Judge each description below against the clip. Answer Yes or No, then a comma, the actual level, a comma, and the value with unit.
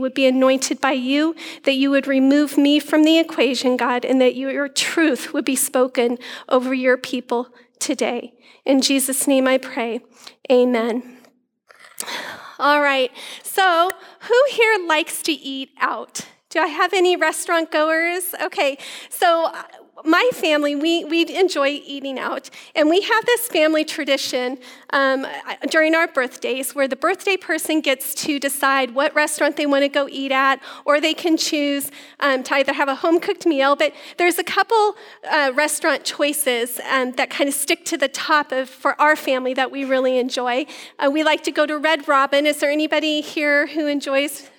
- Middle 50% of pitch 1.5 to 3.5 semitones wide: Yes, average, 3.1 semitones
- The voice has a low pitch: No, very high, 285 Hz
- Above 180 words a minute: No, average, 175 wpm